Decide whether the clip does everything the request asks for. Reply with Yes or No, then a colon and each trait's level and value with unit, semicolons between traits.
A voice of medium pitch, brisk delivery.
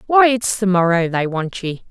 No: high, 195 Hz; fast, 220 wpm